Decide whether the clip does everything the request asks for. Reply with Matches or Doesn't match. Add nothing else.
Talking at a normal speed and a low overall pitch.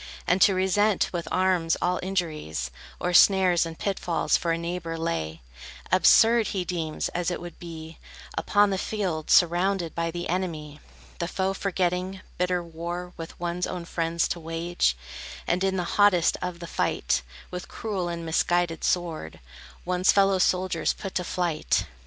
Doesn't match